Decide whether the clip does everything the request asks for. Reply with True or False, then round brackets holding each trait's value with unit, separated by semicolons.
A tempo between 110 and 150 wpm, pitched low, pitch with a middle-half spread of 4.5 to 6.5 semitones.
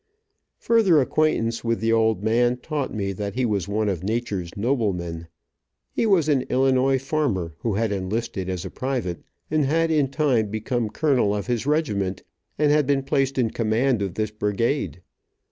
False (170 wpm; 115 Hz; 5.1 semitones)